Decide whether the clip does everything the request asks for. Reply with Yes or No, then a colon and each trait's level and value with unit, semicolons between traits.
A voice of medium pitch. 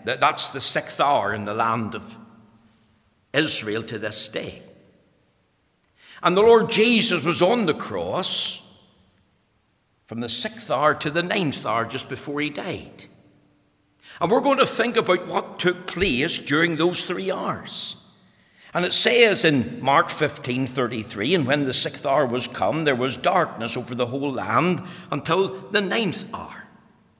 Yes: medium, 145 Hz